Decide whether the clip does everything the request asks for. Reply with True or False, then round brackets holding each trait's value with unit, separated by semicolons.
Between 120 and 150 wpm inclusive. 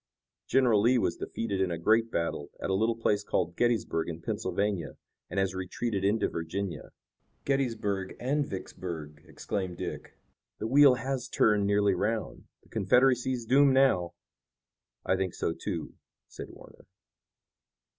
True (145 wpm)